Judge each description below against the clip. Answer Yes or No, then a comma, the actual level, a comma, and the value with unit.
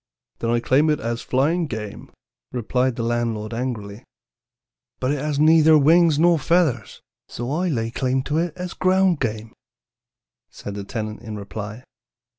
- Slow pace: No, average, 155 wpm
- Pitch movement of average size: No, wide, 5.7 semitones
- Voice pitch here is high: No, low, 130 Hz